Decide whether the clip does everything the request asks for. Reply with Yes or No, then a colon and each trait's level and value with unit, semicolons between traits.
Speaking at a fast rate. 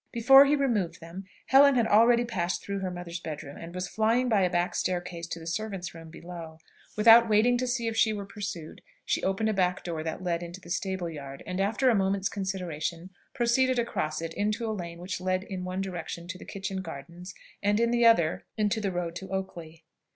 Yes: fast, 215 wpm